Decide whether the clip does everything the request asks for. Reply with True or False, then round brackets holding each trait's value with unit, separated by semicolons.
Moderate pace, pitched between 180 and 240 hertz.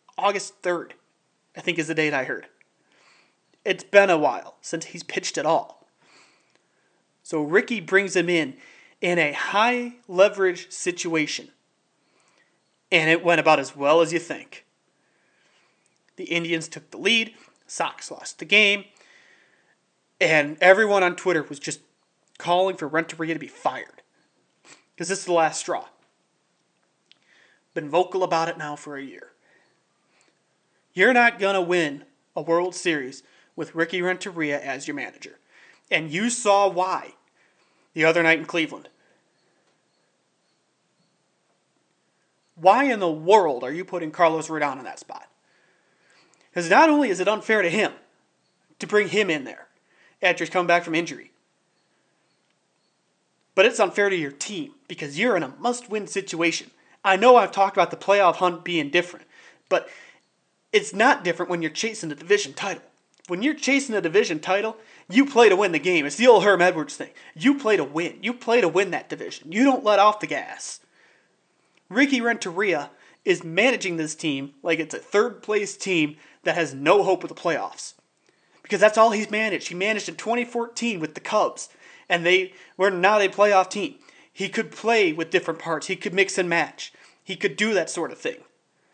True (165 wpm; 185 Hz)